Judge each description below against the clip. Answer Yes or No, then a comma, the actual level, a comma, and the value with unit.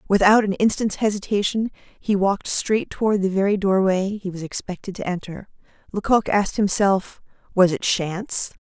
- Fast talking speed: No, average, 145 wpm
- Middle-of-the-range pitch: No, high, 195 Hz